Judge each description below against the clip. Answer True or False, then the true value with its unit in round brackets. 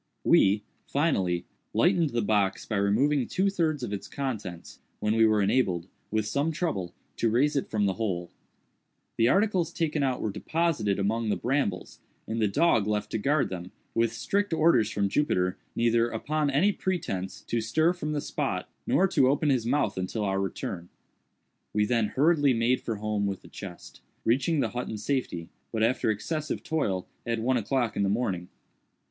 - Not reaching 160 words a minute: False (180 wpm)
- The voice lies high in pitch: False (115 Hz)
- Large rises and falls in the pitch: True (6.2 semitones)